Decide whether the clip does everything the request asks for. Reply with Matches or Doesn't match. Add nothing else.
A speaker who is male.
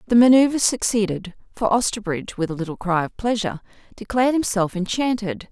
Doesn't match